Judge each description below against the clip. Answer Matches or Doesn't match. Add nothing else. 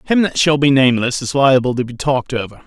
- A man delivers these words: Matches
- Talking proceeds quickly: Matches